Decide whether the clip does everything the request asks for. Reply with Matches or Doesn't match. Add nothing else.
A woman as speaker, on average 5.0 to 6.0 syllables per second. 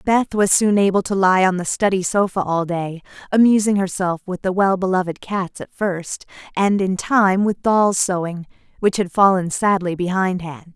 Doesn't match